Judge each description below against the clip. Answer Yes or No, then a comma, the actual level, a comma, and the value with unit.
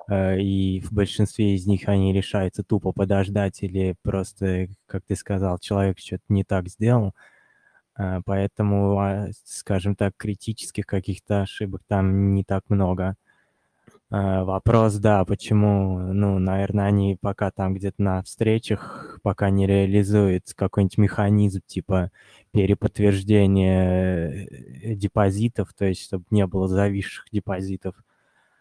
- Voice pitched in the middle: No, low, 100 Hz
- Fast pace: No, average, 115 wpm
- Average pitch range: No, narrow, 1.2 semitones